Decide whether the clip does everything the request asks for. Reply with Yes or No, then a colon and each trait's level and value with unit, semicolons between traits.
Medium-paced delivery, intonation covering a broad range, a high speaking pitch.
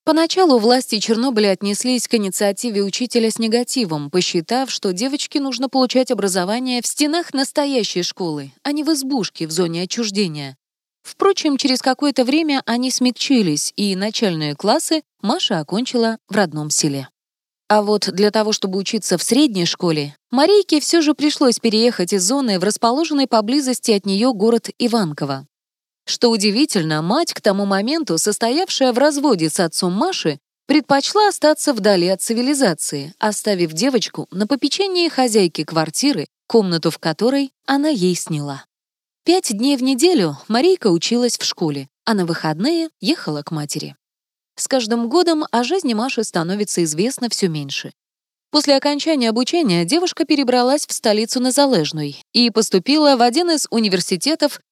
Yes: average, 145 wpm; wide, 6.5 semitones; high, 230 Hz